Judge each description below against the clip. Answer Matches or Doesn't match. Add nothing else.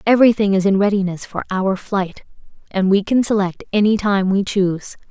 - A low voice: Doesn't match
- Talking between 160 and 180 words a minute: Matches